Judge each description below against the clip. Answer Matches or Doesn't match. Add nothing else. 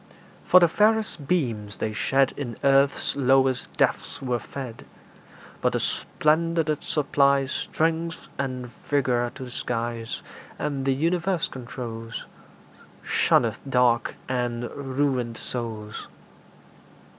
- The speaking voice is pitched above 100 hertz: Matches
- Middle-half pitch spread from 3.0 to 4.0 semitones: Matches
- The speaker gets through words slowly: Matches